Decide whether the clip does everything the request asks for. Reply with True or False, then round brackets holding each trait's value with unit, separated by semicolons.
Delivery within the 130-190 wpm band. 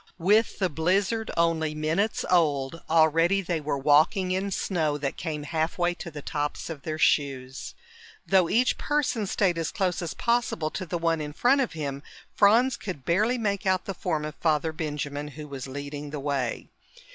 True (180 wpm)